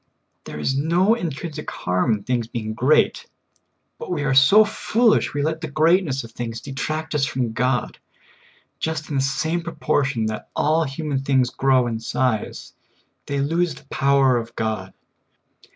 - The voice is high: No, low, 135 Hz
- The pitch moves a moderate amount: Yes, average, 4.6 semitones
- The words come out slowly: No, average, 160 wpm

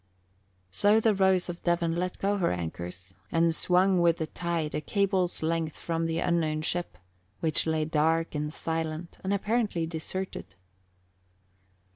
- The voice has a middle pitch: Yes, medium, 165 Hz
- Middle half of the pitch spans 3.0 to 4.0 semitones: No, narrow, 2.6 semitones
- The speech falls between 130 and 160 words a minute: Yes, average, 145 wpm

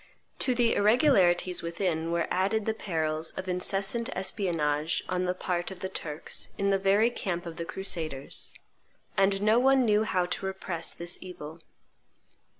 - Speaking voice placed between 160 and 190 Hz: Yes, medium, 185 Hz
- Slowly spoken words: No, average, 155 wpm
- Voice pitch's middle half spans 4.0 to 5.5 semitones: No, average, 3.0 semitones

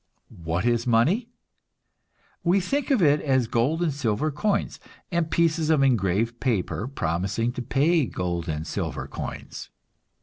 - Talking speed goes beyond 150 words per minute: No, average, 140 wpm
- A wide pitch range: Yes, wide, 7.1 semitones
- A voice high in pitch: No, low, 130 Hz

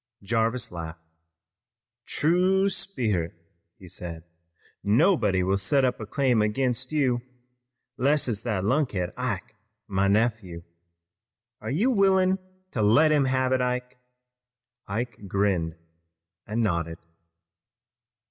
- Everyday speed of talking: No, slow, 110 wpm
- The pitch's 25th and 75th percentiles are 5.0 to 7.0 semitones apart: Yes, wide, 5.6 semitones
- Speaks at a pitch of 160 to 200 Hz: No, low, 115 Hz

